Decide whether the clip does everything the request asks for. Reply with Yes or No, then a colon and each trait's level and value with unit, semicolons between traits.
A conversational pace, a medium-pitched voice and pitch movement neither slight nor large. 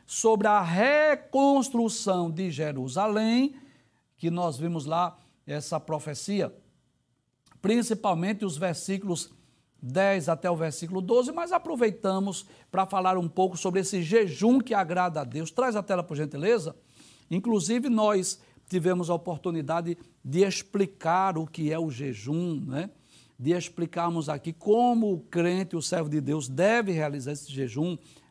Yes: average, 135 wpm; medium, 180 Hz; average, 4.4 semitones